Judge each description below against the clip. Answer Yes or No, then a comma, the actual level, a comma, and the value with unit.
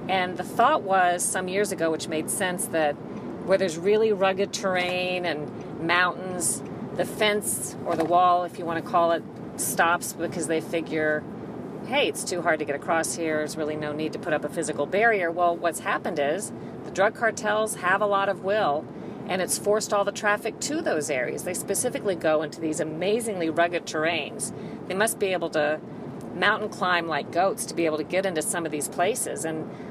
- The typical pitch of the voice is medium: Yes, medium, 175 Hz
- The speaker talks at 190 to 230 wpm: Yes, average, 200 wpm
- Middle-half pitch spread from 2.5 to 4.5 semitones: Yes, average, 3.6 semitones